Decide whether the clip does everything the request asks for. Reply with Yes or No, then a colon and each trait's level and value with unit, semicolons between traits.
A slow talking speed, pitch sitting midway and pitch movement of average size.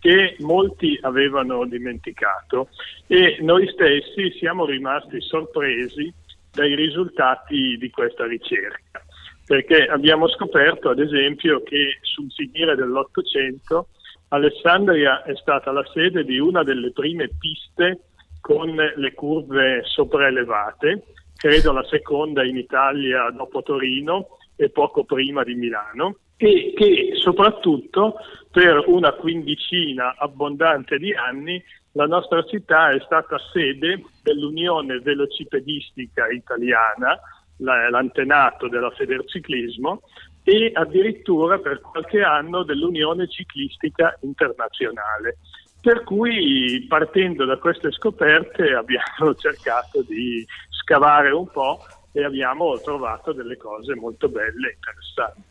No: slow, 110 wpm; medium, 160 Hz; wide, 8.0 semitones